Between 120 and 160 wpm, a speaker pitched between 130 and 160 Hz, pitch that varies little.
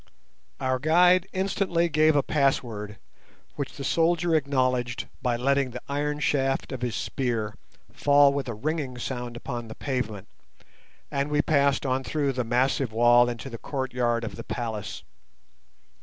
No: average, 150 wpm; low, 135 Hz; average, 3.2 semitones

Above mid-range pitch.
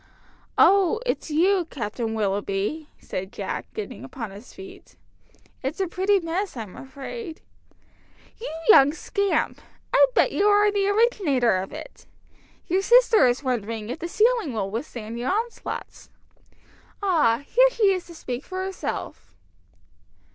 Yes: very high, 330 Hz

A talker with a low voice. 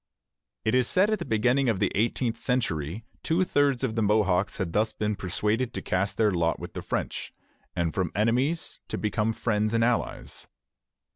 Yes: low, 110 Hz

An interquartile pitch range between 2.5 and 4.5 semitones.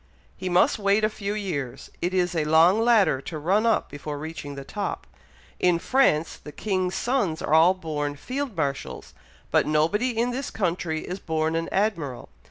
No: average, 5.1 semitones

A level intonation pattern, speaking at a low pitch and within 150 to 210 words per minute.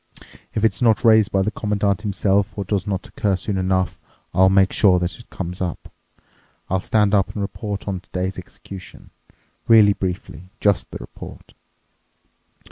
Yes: narrow, 2.0 semitones; low, 100 Hz; average, 155 wpm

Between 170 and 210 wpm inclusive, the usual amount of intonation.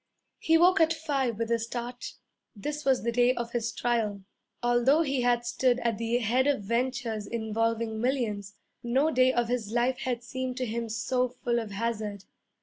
No: average, 180 wpm; narrow, 2.1 semitones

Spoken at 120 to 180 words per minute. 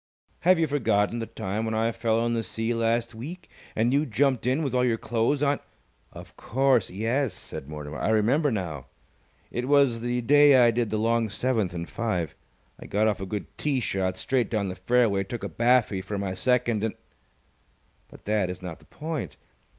No: average, 200 wpm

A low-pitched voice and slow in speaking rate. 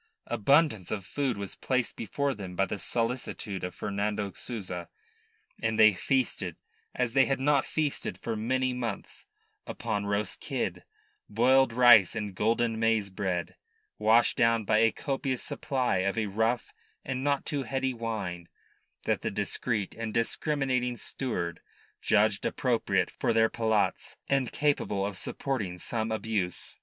No: low, 115 Hz; average, 145 wpm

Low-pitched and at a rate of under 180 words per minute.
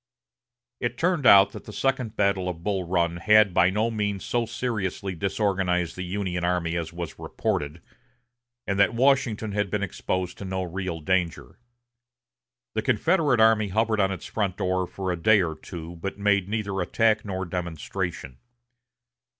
Yes: very low, 95 Hz; average, 160 wpm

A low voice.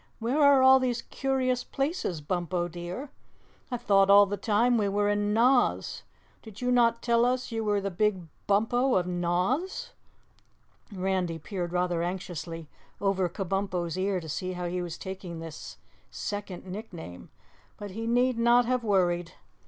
No: high, 200 Hz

